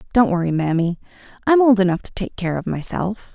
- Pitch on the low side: No, high, 195 Hz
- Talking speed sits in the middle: Yes, average, 195 wpm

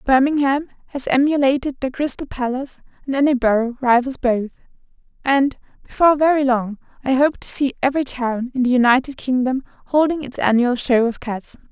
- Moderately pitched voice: No, very high, 260 Hz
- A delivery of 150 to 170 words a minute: Yes, average, 155 wpm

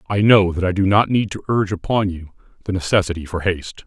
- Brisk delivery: Yes, fast, 235 wpm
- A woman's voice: No, male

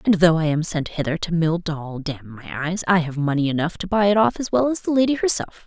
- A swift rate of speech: Yes, fast, 275 wpm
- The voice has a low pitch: No, medium, 175 Hz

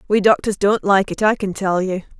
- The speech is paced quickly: Yes, fast, 245 wpm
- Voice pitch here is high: Yes, high, 200 Hz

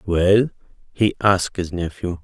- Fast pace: No, slow, 135 wpm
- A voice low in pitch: Yes, very low, 95 Hz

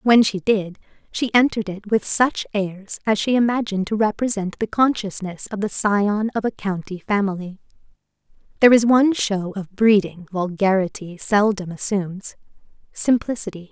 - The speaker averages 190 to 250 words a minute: No, average, 140 wpm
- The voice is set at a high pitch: Yes, high, 205 Hz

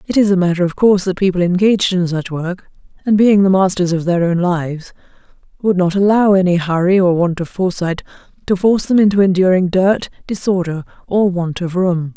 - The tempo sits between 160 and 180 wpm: No, average, 195 wpm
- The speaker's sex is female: Yes, female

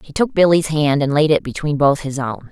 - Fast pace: Yes, fast, 265 wpm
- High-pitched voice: No, medium, 150 Hz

